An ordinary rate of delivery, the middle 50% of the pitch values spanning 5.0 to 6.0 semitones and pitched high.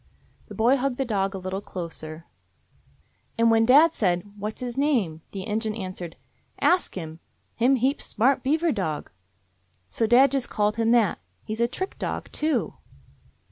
Yes: average, 165 wpm; wide, 5.5 semitones; high, 225 Hz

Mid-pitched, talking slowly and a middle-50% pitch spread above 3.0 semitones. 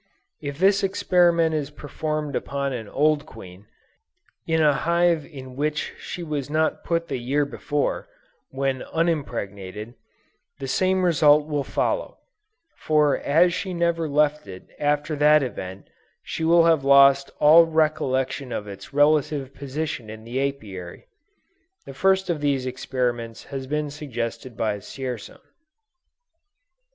Yes: medium, 145 Hz; slow, 130 wpm; average, 3.5 semitones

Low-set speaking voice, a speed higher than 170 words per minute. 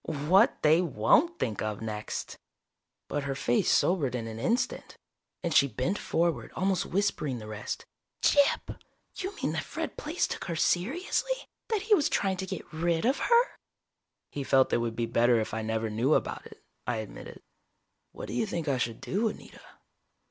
No: medium, 155 Hz; average, 180 wpm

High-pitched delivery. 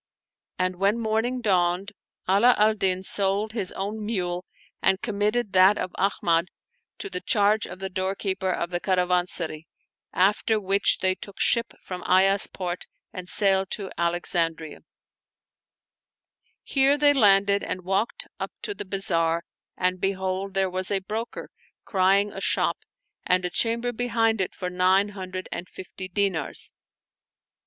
Yes: high, 195 Hz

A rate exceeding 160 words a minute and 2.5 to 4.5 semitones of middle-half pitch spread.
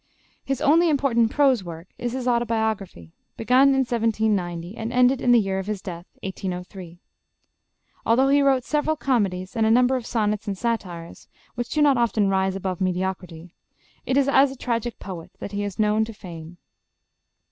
No: average, 180 wpm; average, 5.0 semitones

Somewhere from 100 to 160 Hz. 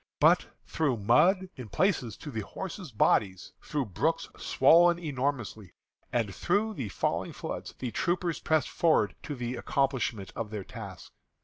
Yes: low, 135 Hz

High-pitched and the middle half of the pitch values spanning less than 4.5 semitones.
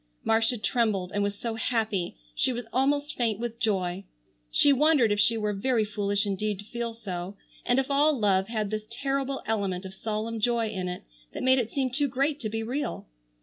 Yes: high, 225 Hz; average, 3.8 semitones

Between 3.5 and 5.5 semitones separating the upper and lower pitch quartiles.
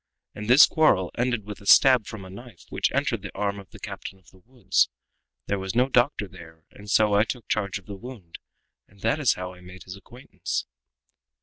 Yes: average, 4.3 semitones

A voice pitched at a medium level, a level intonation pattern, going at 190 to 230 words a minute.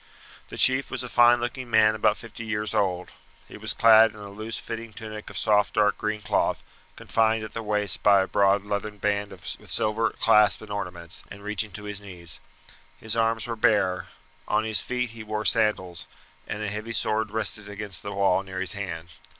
No: low, 105 Hz; narrow, 1.7 semitones; average, 200 wpm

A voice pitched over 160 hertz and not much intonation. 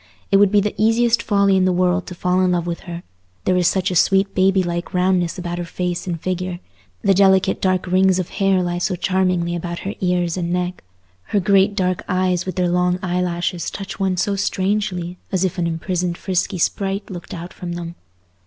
Yes: medium, 185 Hz; narrow, 1.5 semitones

